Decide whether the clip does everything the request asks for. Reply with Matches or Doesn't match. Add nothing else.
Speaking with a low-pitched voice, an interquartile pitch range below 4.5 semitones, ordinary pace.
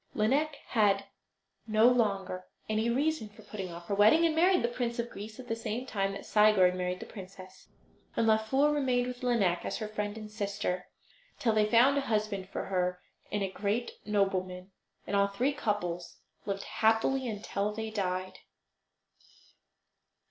Doesn't match